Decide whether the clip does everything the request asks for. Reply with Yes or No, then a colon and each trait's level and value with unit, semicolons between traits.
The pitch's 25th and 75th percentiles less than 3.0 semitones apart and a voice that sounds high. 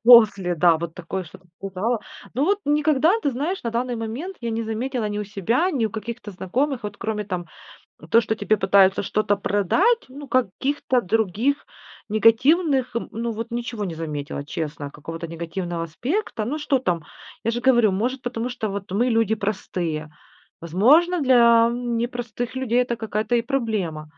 No: average, 4.7 semitones; high, 225 Hz